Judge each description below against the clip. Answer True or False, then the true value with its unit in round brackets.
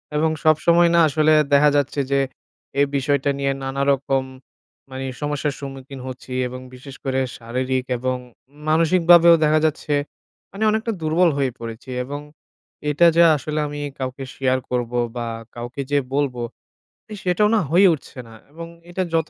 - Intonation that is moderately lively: True (3.4 semitones)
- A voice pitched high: False (140 Hz)